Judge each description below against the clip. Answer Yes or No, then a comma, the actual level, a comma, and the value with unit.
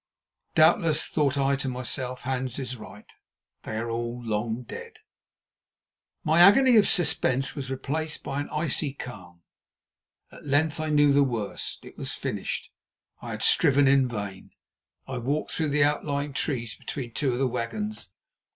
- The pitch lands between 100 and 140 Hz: Yes, low, 135 Hz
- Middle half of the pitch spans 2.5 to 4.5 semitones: Yes, average, 3.7 semitones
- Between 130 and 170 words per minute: Yes, average, 155 wpm